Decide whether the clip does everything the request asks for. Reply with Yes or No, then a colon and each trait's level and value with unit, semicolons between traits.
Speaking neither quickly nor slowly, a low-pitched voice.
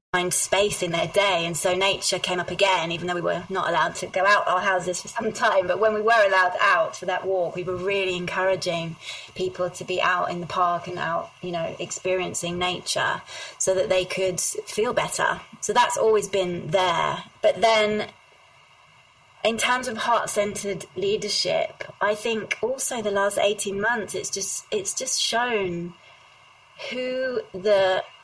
No: average, 180 wpm; high, 195 Hz